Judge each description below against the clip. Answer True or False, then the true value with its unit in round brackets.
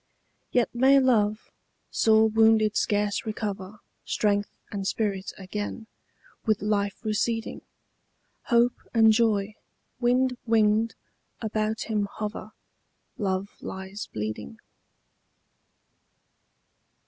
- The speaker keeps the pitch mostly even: True (1.8 semitones)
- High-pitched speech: True (215 Hz)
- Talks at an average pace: False (90 wpm)